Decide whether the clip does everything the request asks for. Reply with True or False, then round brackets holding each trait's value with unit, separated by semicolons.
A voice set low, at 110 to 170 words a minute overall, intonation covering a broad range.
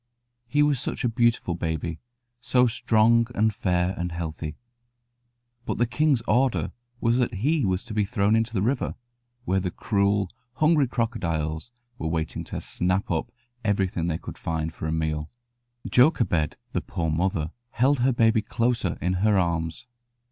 True (105 Hz; 160 wpm; 6.1 semitones)